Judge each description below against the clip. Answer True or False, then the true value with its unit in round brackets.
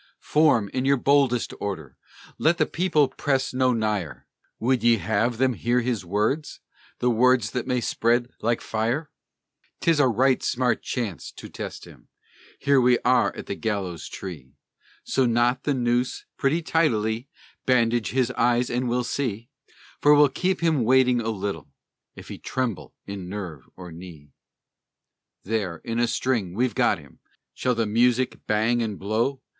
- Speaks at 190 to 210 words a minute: False (160 wpm)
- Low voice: True (120 Hz)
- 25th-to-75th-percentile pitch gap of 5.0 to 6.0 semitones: False (3.5 semitones)